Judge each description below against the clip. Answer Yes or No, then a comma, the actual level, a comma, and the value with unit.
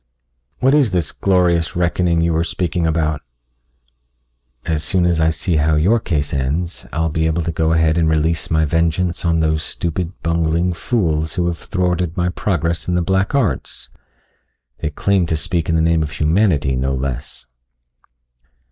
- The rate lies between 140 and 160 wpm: No, average, 170 wpm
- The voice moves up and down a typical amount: No, narrow, 2.1 semitones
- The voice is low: Yes, very low, 85 Hz